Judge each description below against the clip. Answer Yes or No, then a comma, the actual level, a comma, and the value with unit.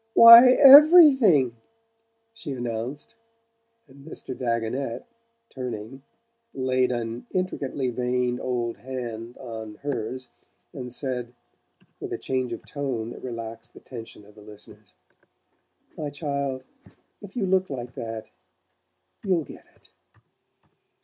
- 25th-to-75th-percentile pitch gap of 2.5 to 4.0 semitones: Yes, average, 3.5 semitones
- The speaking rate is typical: No, slow, 115 wpm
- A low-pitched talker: Yes, low, 125 Hz